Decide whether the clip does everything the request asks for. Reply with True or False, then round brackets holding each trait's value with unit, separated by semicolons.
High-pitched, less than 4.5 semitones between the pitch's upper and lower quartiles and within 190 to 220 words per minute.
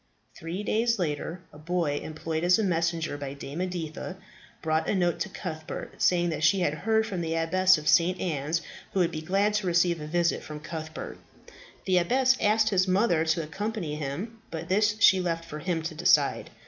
False (170 Hz; 3.0 semitones; 200 wpm)